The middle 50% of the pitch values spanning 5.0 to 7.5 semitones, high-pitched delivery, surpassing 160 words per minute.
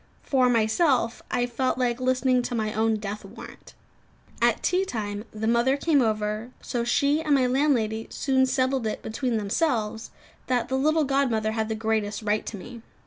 No: average, 3.3 semitones; high, 240 Hz; average, 175 wpm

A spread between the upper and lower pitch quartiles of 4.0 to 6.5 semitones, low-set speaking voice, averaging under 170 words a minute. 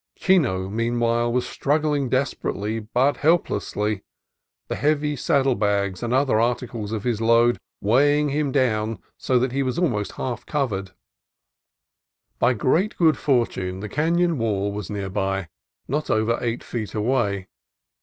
Yes: average, 4.8 semitones; low, 120 Hz; average, 140 wpm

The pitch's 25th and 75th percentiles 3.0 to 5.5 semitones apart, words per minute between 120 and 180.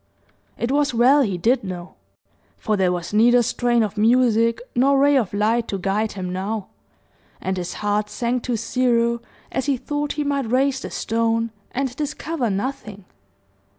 Yes: average, 3.9 semitones; average, 165 wpm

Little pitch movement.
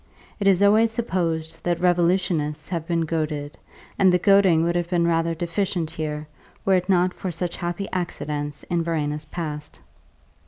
Yes: narrow, 2.3 semitones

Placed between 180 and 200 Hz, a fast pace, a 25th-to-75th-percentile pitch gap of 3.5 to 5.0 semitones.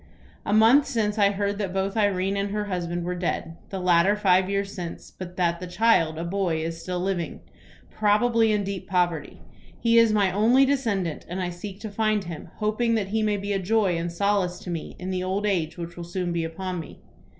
No: high, 190 Hz; fast, 215 wpm; average, 3.0 semitones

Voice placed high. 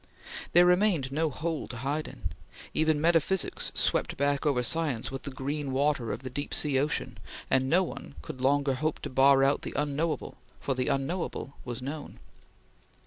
No: medium, 140 Hz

